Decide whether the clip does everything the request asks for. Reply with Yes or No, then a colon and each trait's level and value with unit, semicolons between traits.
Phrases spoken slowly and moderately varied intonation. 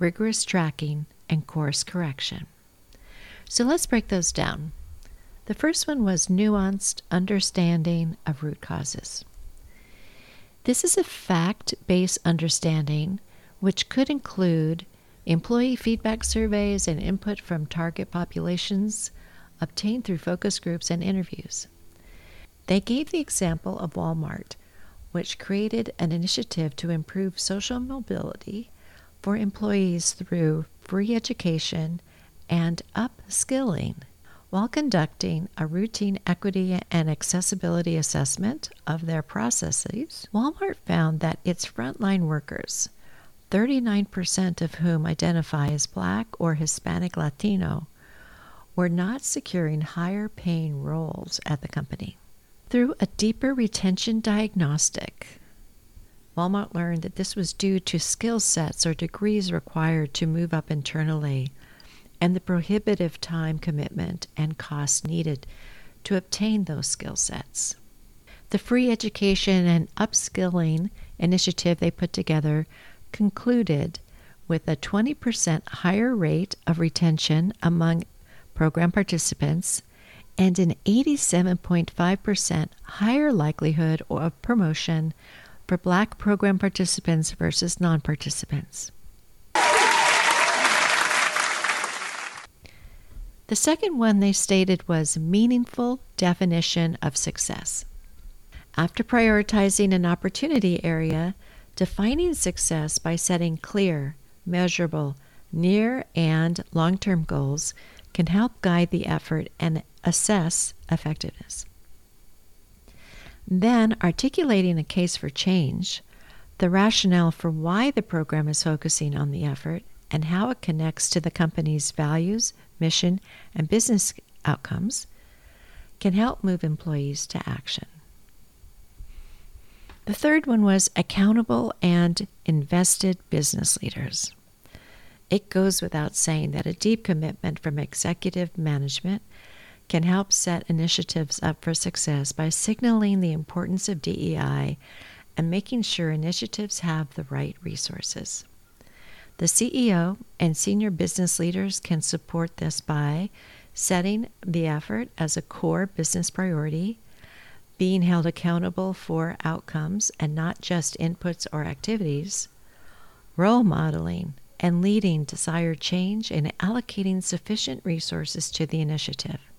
Yes: slow, 110 wpm; average, 3.9 semitones